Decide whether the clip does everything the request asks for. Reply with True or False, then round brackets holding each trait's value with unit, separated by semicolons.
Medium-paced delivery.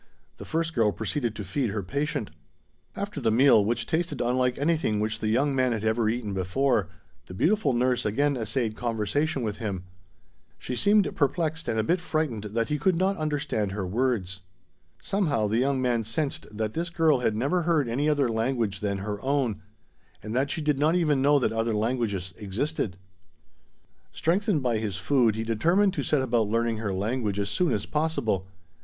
True (185 wpm)